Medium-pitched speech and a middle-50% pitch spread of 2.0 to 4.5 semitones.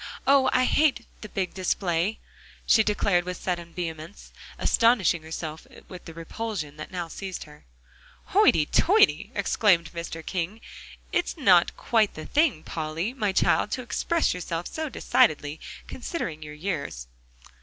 No: medium, 180 Hz; wide, 5.5 semitones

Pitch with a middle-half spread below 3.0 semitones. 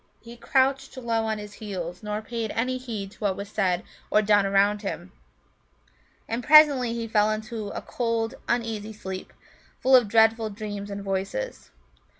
Yes: narrow, 2.6 semitones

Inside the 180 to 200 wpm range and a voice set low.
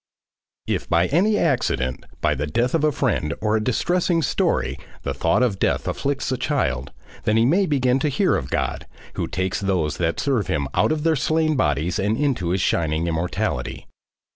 Yes: average, 185 wpm; low, 110 Hz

